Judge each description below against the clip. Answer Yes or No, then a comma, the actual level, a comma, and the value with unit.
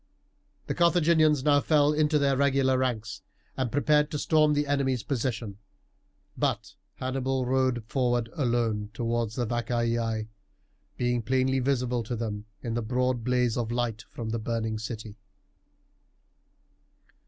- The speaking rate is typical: No, slow, 130 wpm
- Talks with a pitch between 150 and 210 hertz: No, low, 125 Hz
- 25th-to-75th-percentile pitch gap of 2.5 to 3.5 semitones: Yes, average, 3.0 semitones